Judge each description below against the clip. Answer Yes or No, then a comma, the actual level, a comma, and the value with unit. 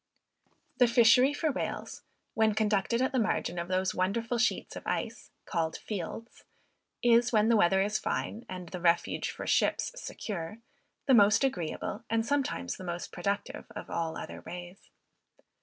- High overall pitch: Yes, high, 210 Hz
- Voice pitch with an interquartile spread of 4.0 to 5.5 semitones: Yes, average, 4.6 semitones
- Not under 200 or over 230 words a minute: No, average, 155 wpm